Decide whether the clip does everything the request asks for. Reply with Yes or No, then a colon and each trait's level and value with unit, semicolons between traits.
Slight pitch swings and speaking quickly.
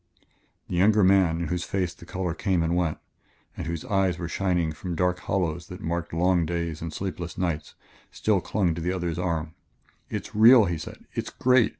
No: narrow, 2.1 semitones; average, 195 wpm